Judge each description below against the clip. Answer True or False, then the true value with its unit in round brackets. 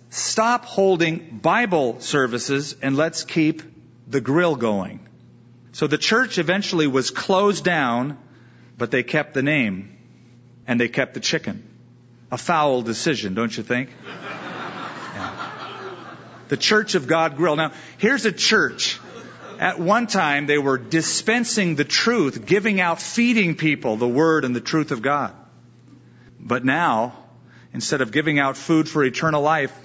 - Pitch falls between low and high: True (145 Hz)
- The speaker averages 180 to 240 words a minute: False (145 wpm)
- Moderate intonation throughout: False (5.8 semitones)